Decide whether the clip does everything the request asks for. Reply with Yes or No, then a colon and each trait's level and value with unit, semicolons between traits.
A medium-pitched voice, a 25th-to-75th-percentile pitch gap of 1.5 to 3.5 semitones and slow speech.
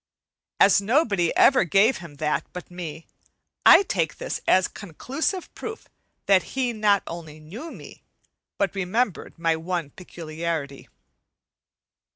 No: medium, 180 Hz; average, 4.8 semitones; slow, 125 wpm